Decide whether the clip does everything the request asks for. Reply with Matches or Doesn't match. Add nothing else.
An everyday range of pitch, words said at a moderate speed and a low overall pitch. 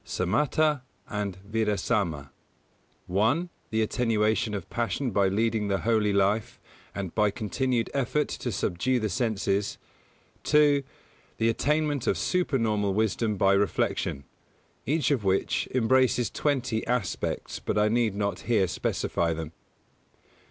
Doesn't match